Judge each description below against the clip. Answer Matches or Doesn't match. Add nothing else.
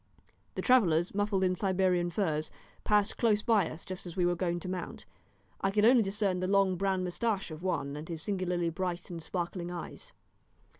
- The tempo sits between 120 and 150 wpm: Doesn't match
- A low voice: Doesn't match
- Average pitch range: Doesn't match